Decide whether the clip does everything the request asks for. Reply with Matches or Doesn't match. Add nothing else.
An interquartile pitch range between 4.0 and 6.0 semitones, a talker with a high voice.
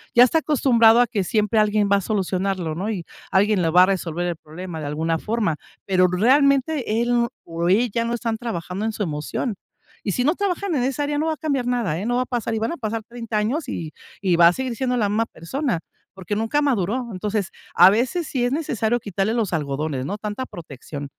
Matches